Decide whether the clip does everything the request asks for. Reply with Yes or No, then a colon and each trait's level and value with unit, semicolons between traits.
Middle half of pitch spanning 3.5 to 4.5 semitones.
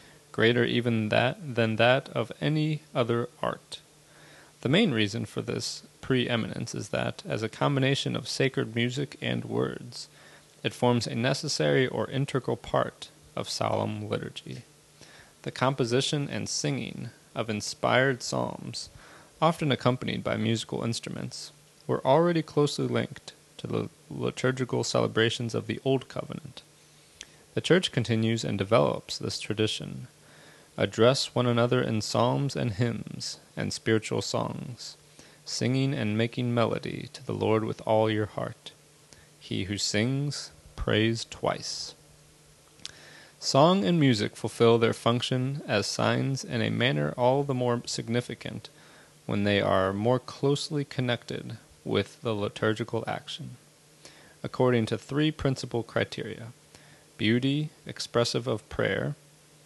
Yes: average, 4.0 semitones